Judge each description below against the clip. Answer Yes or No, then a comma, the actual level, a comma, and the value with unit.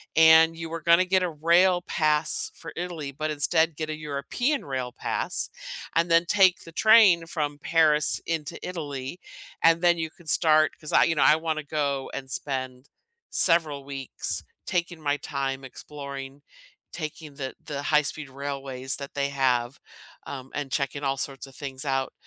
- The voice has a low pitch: No, medium, 150 Hz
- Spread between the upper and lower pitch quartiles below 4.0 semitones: Yes, average, 3.2 semitones